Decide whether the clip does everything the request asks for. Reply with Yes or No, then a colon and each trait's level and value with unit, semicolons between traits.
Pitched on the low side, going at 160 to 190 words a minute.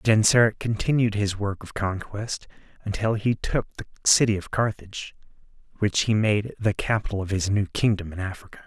Yes: low, 105 Hz; average, 165 wpm